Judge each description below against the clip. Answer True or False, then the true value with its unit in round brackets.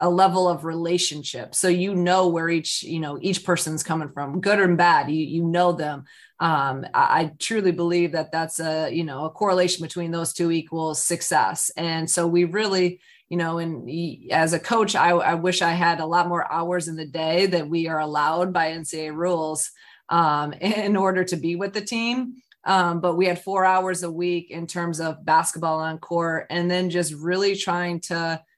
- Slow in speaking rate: False (200 wpm)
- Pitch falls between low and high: True (170 Hz)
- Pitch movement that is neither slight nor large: False (1.9 semitones)